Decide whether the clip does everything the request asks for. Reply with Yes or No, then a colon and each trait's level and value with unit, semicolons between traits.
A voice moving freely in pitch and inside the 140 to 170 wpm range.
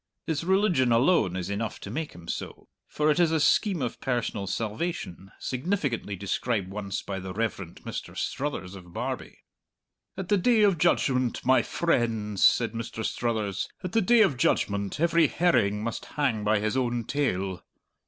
Yes: wide, 8.0 semitones; average, 165 wpm